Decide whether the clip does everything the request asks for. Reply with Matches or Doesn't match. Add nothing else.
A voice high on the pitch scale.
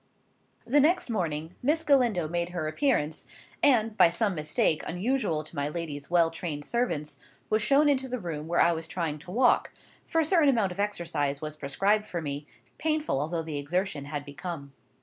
Doesn't match